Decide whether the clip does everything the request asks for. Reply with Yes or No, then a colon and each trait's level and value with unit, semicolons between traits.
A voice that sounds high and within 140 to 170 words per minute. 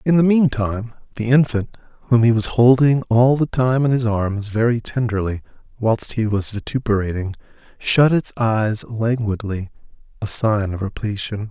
No: low, 115 Hz; average, 150 wpm